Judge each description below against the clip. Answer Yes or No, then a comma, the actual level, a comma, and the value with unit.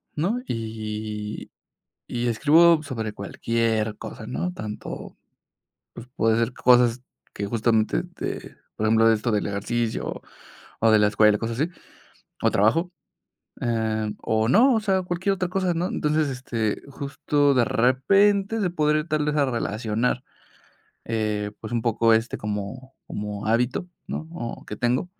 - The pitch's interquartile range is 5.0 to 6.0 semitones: Yes, wide, 5.6 semitones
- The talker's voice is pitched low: Yes, low, 120 Hz